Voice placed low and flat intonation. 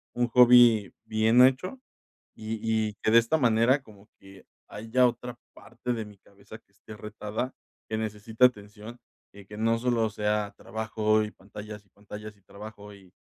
Yes: low, 110 Hz; narrow, 2.0 semitones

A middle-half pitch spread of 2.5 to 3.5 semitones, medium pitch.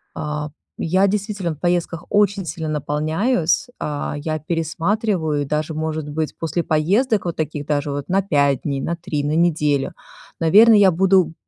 No: average, 4.0 semitones; medium, 160 Hz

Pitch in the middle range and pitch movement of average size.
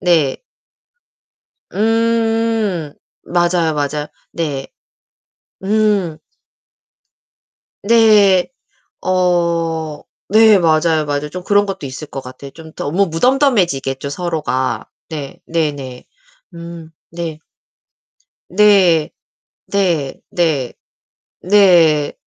Yes: medium, 170 Hz; average, 4.9 semitones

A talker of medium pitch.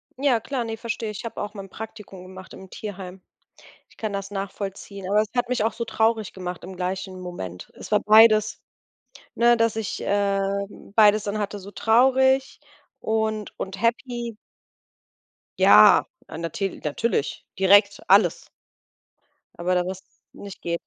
No: high, 205 Hz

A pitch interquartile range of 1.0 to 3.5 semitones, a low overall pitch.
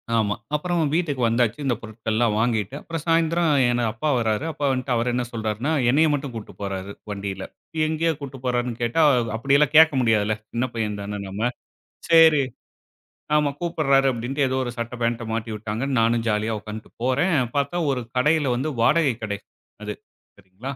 No: average, 4.7 semitones; low, 120 Hz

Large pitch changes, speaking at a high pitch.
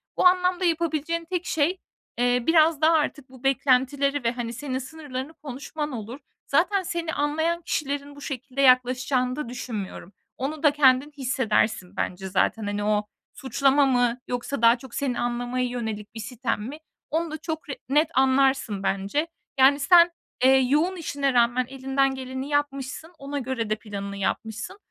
No: average, 3.4 semitones; very high, 265 Hz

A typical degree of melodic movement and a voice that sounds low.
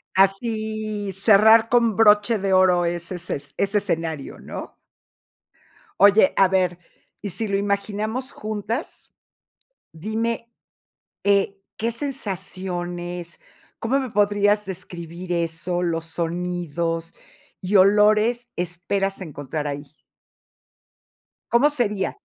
No: average, 3.6 semitones; high, 195 Hz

